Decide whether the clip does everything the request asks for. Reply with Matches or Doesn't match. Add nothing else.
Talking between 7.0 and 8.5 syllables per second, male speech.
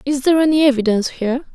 Doesn't match